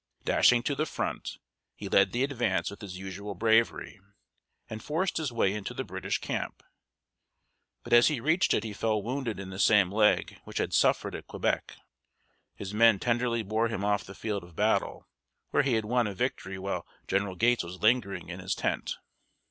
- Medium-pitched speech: No, low, 110 Hz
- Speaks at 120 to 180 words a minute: No, average, 190 wpm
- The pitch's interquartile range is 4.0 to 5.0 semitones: No, average, 3.5 semitones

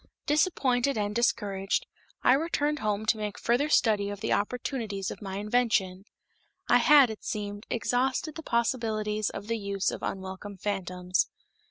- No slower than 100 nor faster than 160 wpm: Yes, average, 155 wpm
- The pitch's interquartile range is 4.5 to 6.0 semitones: No, average, 3.6 semitones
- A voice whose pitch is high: Yes, high, 215 Hz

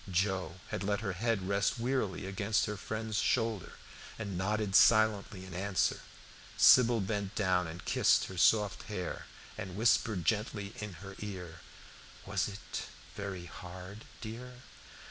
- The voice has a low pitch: Yes, low, 100 Hz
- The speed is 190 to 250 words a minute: No, average, 140 wpm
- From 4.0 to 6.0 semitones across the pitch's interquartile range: No, narrow, 2.6 semitones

